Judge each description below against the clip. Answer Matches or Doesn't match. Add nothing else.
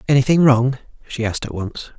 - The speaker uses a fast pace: Doesn't match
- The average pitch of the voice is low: Matches